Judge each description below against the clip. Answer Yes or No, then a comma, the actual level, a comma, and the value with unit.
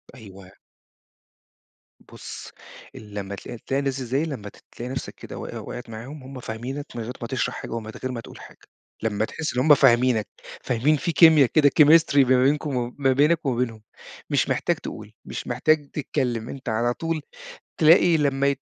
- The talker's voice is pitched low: Yes, low, 130 Hz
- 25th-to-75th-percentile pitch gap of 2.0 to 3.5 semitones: No, average, 3.9 semitones